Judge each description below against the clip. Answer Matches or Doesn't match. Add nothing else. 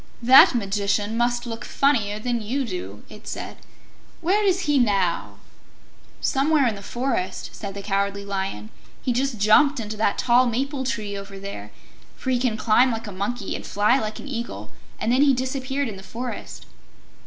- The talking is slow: Doesn't match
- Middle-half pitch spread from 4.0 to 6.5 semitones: Matches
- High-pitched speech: Matches